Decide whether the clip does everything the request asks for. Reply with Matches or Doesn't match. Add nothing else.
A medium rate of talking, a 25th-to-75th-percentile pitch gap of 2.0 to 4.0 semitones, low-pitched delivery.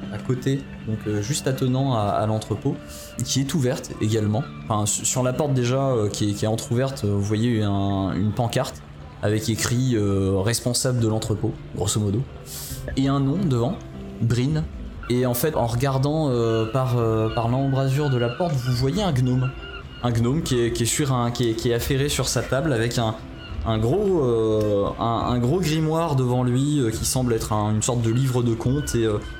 Matches